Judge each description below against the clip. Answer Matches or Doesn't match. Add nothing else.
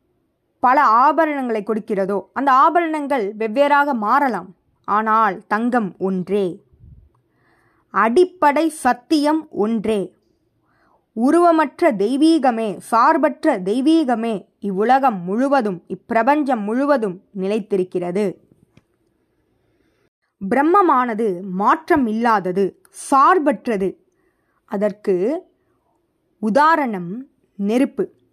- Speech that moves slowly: Matches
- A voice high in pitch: Matches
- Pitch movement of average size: Doesn't match